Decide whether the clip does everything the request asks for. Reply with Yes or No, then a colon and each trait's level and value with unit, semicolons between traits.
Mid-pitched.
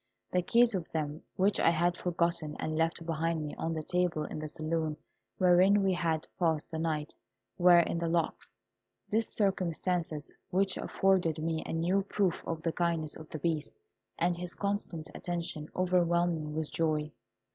Yes: medium, 170 Hz